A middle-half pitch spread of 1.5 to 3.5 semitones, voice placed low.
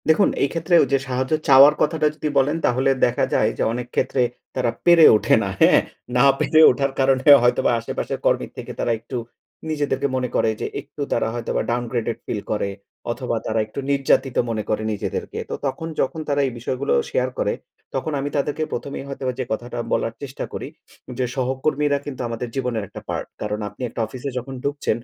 Yes: average, 2.9 semitones; low, 130 Hz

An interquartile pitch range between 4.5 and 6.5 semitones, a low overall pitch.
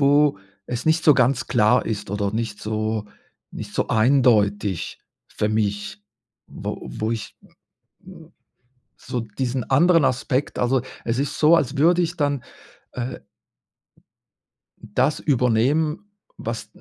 Yes: average, 4.8 semitones; low, 125 Hz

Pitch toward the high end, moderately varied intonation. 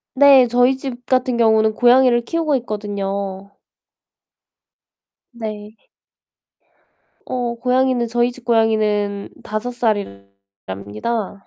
Yes: high, 230 Hz; average, 3.4 semitones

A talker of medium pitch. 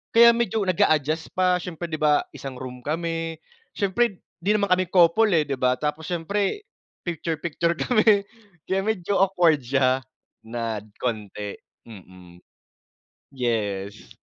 Yes: medium, 160 Hz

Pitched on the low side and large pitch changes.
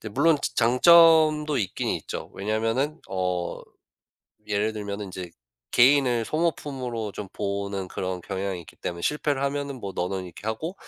Yes: low, 110 Hz; wide, 6.7 semitones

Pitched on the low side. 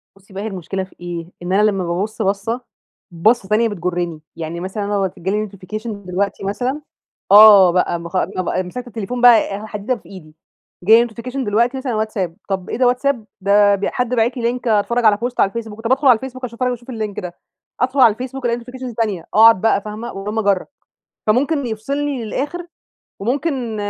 No: high, 215 Hz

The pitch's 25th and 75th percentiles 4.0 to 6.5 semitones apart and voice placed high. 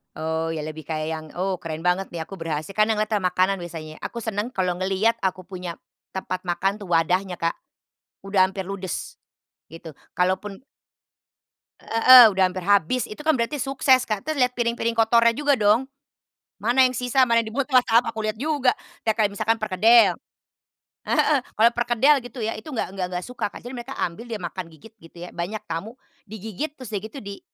Yes: average, 4.7 semitones; high, 210 Hz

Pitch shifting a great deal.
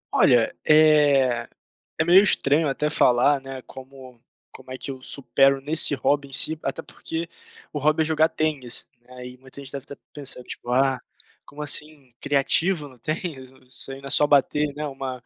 No: narrow, 2.6 semitones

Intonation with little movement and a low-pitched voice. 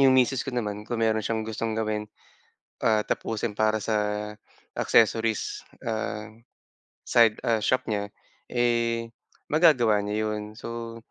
Yes: narrow, 1.6 semitones; low, 110 Hz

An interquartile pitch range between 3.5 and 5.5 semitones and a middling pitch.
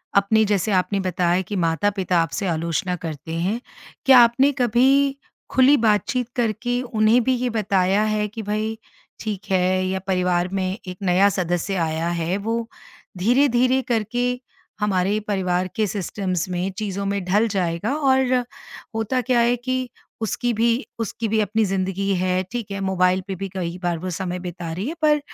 No: average, 4.2 semitones; high, 200 Hz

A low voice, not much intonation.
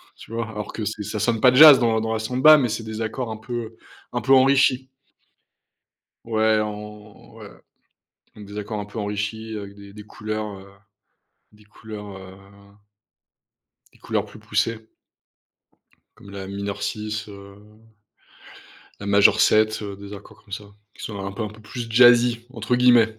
Yes: low, 110 Hz; narrow, 2.0 semitones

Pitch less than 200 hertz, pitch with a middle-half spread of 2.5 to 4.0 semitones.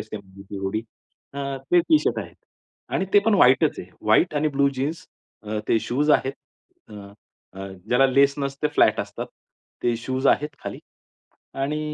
No: low, 135 Hz; wide, 5.5 semitones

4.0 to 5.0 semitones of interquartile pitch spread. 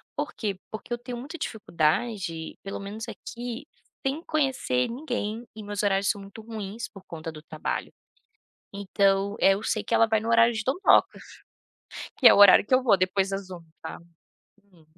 No: average, 3.3 semitones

